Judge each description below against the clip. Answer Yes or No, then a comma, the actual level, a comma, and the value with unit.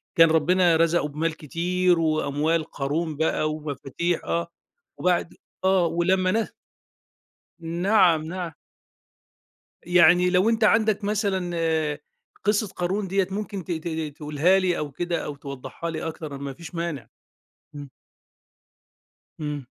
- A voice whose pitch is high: No, medium, 170 Hz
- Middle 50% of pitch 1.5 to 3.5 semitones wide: Yes, average, 3.0 semitones